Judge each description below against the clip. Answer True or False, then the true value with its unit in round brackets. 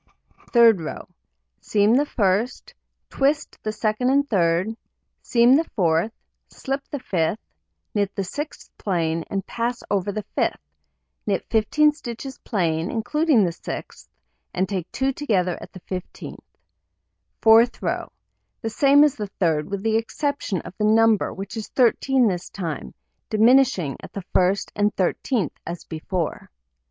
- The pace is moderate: True (145 wpm)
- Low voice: False (215 Hz)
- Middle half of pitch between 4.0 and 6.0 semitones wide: True (5.2 semitones)